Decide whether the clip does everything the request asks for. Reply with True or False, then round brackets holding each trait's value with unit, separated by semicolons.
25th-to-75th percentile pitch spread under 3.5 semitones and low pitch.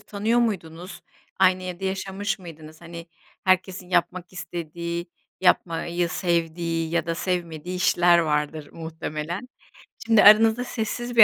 False (2.4 semitones; 175 Hz)